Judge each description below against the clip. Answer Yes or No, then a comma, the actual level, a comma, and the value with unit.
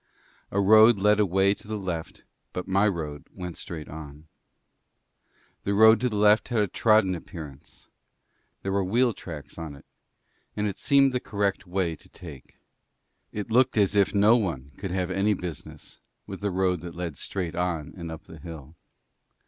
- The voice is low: Yes, very low, 95 Hz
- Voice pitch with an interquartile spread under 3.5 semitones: No, average, 3.9 semitones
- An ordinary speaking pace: Yes, average, 175 wpm